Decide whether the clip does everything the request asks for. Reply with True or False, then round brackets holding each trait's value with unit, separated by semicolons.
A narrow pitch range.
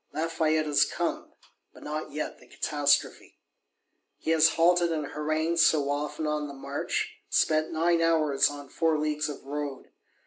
True (1.8 semitones)